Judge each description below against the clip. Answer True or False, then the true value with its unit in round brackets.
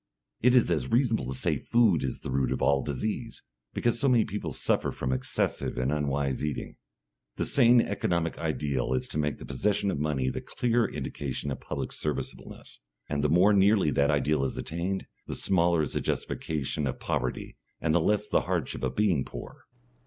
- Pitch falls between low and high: False (75 Hz)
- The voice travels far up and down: True (6.8 semitones)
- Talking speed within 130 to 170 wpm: False (190 wpm)